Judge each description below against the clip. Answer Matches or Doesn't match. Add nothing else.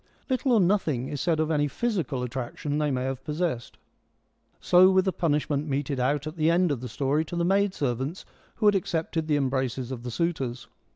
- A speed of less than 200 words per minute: Doesn't match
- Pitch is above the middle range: Doesn't match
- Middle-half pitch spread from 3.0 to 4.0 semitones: Doesn't match